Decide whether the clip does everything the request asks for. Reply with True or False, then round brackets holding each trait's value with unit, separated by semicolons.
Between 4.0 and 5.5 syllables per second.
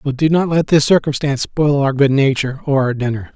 False (5.9 syllables/s)